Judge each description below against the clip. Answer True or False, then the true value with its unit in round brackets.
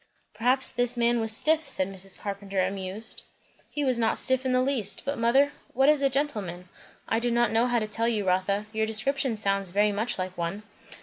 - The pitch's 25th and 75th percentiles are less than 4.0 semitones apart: False (4.3 semitones)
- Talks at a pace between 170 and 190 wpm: False (205 wpm)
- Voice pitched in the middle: False (225 Hz)